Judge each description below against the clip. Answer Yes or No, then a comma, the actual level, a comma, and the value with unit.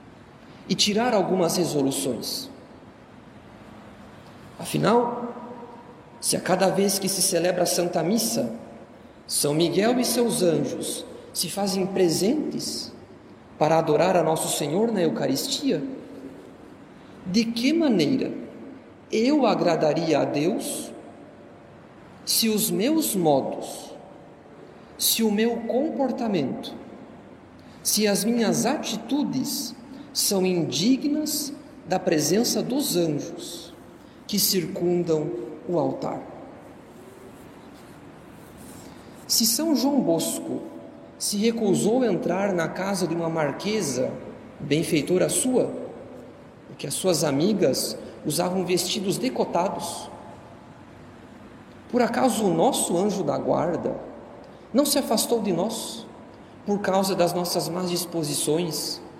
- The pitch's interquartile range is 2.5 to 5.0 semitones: No, wide, 5.6 semitones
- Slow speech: Yes, slow, 100 wpm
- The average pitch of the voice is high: Yes, high, 200 Hz